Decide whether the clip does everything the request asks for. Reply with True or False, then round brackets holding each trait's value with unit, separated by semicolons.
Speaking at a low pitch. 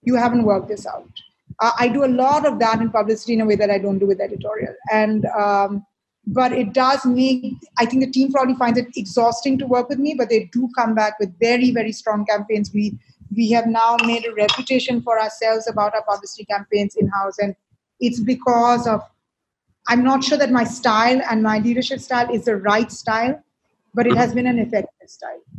False (230 Hz)